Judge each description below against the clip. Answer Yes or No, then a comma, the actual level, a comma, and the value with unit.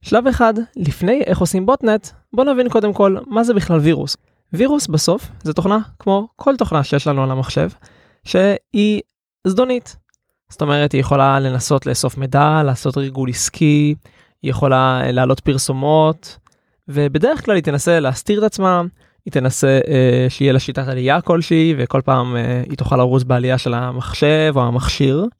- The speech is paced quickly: Yes, fast, 160 wpm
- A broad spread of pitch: Yes, wide, 6.6 semitones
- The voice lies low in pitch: No, medium, 150 Hz